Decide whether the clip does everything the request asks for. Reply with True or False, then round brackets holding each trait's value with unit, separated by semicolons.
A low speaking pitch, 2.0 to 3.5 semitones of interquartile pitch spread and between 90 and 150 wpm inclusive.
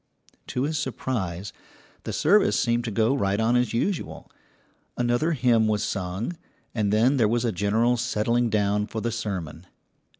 False (115 Hz; 3.0 semitones; 160 wpm)